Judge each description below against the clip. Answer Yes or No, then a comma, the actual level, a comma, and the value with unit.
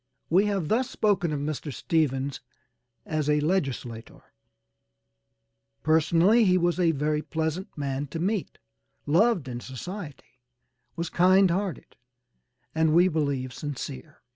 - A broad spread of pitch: No, average, 4.3 semitones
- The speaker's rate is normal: No, slow, 120 wpm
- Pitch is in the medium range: Yes, medium, 160 Hz